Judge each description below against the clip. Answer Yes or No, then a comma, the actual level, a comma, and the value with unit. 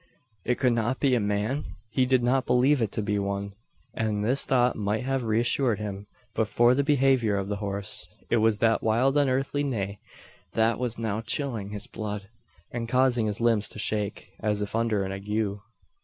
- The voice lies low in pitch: Yes, low, 115 Hz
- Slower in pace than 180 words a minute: No, average, 190 wpm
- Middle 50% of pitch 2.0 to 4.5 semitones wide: Yes, average, 3.5 semitones